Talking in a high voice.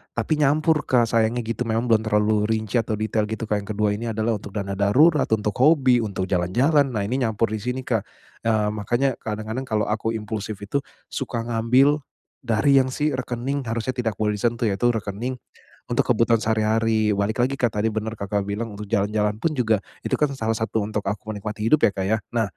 No: low, 110 Hz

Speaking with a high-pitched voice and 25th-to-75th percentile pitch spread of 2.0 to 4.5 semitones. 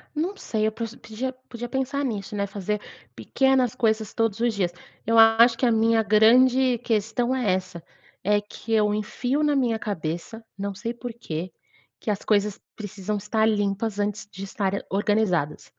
Yes: high, 220 Hz; average, 2.8 semitones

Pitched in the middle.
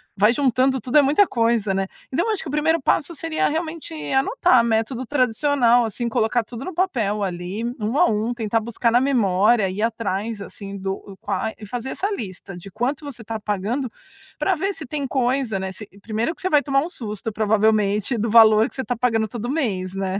No: high, 230 Hz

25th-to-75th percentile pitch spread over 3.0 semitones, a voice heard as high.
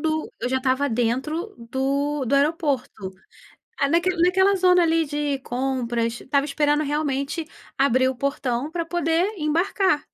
Yes: average, 3.8 semitones; very high, 285 Hz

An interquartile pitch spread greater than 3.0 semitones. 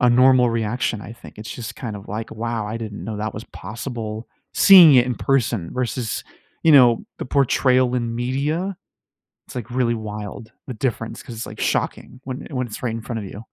No: average, 2.7 semitones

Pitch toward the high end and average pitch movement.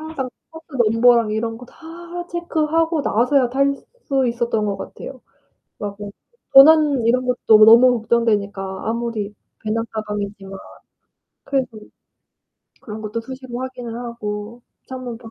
Yes: high, 235 Hz; average, 3.2 semitones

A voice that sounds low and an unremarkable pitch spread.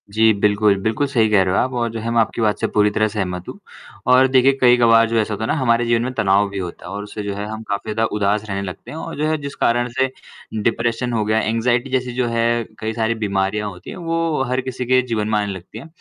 Yes: low, 110 Hz; average, 3.1 semitones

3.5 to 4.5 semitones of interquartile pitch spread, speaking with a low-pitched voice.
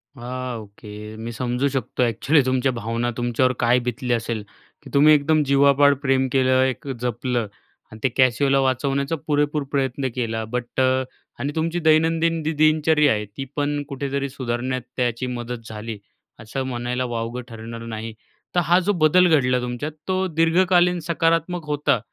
Yes: average, 3.8 semitones; low, 130 Hz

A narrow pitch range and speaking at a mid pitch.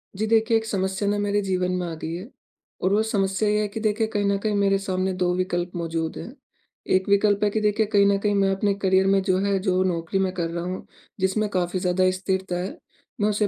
No: narrow, 2.0 semitones; high, 195 Hz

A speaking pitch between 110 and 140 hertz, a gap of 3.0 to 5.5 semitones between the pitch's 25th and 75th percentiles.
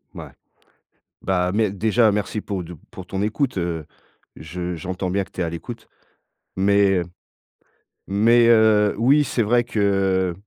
No: low, 100 Hz; average, 3.3 semitones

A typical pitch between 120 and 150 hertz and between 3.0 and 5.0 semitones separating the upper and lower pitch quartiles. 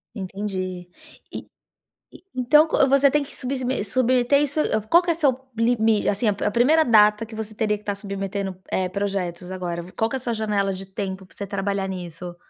No: high, 210 Hz; average, 4.7 semitones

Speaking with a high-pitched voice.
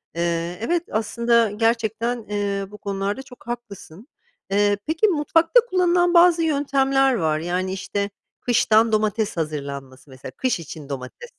Yes: high, 215 Hz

